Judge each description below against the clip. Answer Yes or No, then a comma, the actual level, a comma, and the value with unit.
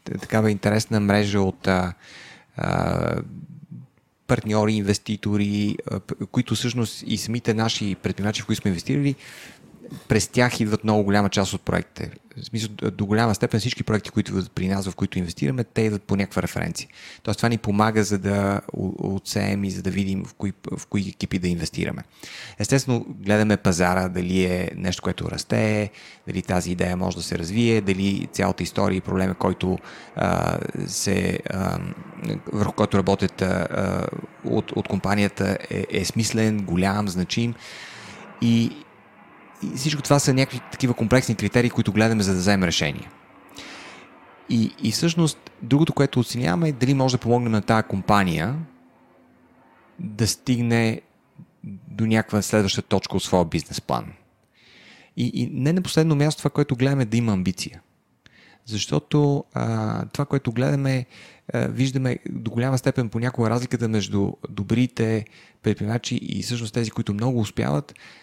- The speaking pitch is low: Yes, low, 110 Hz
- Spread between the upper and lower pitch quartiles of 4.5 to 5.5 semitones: No, average, 3.7 semitones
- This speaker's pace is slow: No, average, 150 wpm